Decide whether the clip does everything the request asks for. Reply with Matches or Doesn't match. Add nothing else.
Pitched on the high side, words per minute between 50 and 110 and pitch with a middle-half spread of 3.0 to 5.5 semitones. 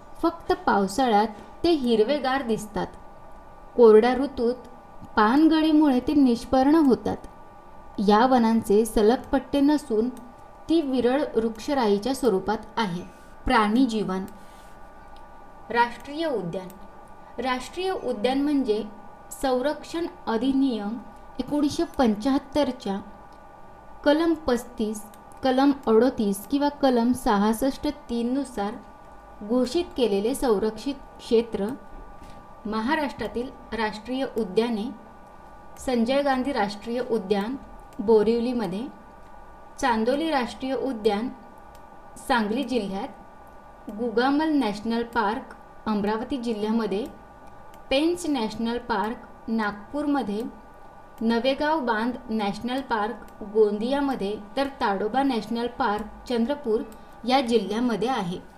Matches